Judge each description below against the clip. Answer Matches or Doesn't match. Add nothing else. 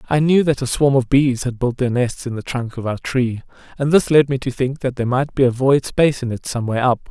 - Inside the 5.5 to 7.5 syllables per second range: Matches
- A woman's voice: Doesn't match